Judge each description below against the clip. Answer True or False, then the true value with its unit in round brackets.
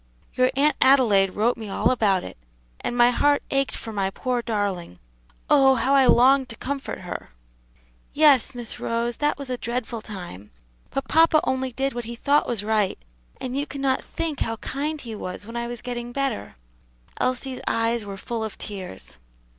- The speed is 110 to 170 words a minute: False (180 wpm)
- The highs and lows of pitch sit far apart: False (3.9 semitones)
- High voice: True (240 Hz)